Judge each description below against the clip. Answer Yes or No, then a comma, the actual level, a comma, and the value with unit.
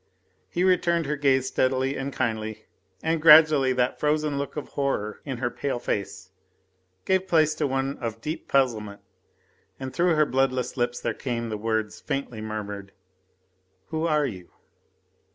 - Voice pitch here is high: No, low, 135 Hz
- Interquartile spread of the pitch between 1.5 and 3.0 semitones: No, average, 4.9 semitones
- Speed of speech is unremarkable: Yes, average, 150 wpm